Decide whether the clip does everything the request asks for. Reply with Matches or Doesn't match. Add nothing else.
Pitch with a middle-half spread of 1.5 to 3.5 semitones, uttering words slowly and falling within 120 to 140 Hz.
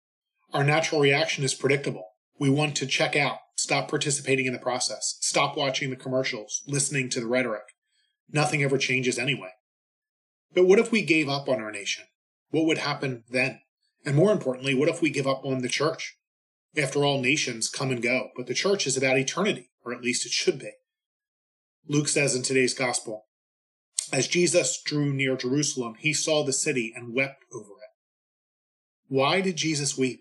Doesn't match